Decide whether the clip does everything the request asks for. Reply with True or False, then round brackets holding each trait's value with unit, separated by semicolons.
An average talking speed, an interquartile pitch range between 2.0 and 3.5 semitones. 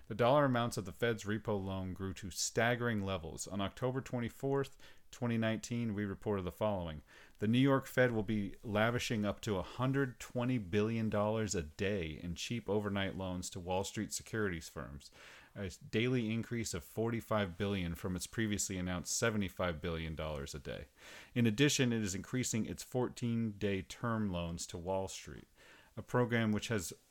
False (160 wpm; 3.9 semitones)